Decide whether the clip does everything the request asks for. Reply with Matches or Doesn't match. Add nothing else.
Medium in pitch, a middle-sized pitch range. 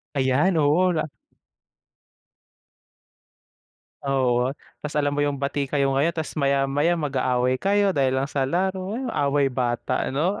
Matches